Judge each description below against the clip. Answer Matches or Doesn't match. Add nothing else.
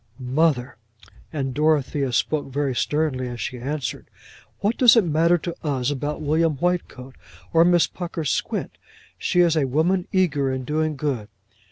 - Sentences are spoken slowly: Doesn't match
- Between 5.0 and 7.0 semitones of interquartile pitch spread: Doesn't match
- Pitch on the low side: Doesn't match